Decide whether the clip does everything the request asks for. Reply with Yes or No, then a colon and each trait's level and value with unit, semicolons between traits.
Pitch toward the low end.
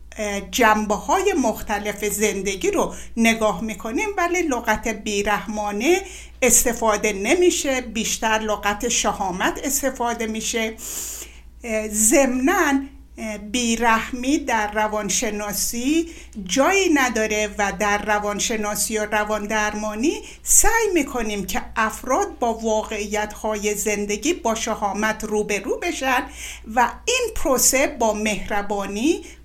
No: high, 220 Hz